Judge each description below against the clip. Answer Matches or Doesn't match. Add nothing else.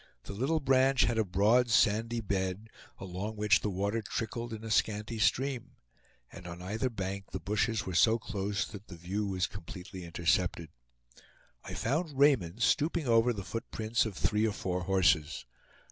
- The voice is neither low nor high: Doesn't match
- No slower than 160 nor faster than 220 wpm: Matches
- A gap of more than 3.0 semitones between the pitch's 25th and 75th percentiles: Matches